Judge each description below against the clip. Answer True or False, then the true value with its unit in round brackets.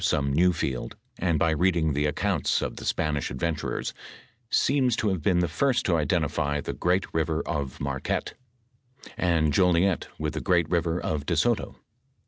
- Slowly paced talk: False (165 wpm)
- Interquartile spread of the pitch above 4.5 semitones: False (3.3 semitones)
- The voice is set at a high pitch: False (80 Hz)